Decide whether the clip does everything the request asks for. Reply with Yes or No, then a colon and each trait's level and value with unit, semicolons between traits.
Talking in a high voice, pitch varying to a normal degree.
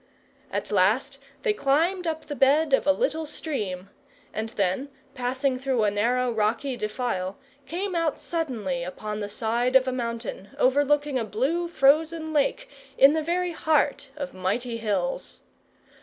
No: very high, 265 Hz; wide, 6.1 semitones